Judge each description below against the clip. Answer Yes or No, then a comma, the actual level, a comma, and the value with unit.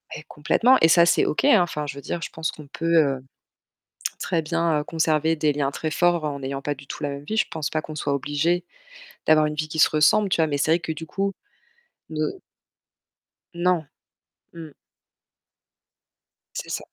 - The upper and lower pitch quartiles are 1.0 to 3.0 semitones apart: Yes, narrow, 2.4 semitones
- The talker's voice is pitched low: No, medium, 155 Hz